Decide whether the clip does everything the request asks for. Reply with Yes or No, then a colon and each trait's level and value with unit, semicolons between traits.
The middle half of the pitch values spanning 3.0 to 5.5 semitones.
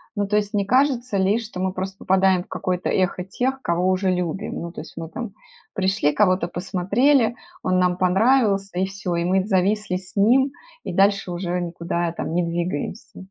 No: narrow, 2.6 semitones